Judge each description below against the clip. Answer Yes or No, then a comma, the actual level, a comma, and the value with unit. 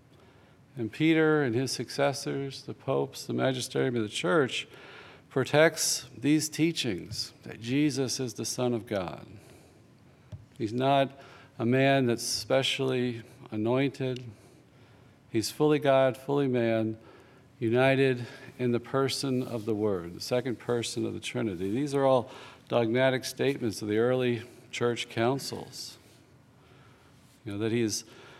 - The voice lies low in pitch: Yes, low, 125 Hz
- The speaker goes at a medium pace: No, slow, 130 wpm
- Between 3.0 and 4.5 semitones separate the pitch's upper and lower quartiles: No, narrow, 2.6 semitones